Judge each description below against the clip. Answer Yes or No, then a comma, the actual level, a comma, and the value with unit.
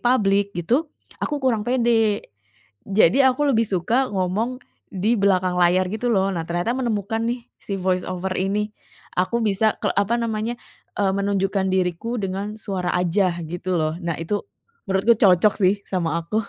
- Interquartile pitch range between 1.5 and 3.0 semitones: No, average, 3.5 semitones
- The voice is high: Yes, high, 200 Hz